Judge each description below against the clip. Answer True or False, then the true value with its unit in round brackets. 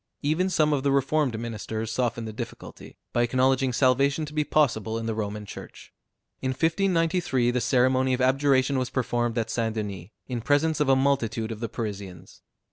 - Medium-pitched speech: False (130 Hz)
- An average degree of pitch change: True (3.7 semitones)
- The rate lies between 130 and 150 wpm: False (180 wpm)